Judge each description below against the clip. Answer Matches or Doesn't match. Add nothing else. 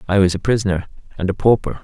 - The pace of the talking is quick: Matches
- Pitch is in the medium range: Doesn't match